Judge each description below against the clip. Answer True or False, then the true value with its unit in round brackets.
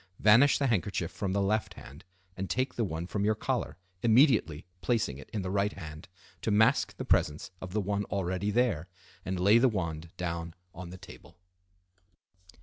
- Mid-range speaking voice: False (100 Hz)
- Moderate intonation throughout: True (4.2 semitones)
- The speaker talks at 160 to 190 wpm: True (180 wpm)